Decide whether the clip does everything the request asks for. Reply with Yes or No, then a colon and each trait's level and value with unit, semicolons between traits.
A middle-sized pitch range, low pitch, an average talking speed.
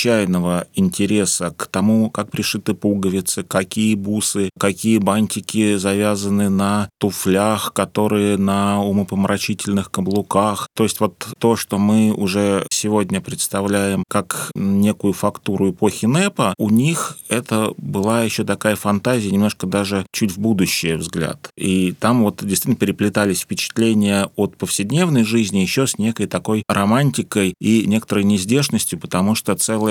No: narrow, 1.8 semitones; low, 105 Hz; average, 130 wpm